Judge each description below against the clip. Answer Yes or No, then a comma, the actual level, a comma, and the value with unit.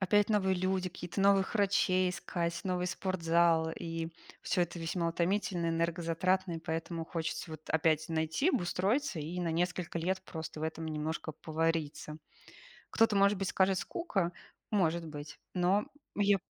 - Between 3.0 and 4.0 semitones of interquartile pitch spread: No, narrow, 2.6 semitones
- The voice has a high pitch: No, medium, 175 Hz